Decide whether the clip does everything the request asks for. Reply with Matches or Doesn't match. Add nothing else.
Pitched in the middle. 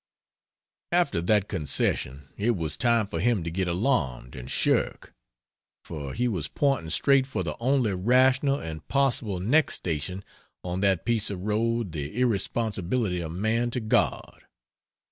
Doesn't match